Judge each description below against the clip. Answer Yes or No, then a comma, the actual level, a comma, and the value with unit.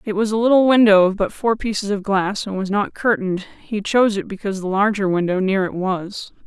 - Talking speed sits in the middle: No, fast, 230 wpm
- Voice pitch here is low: No, high, 200 Hz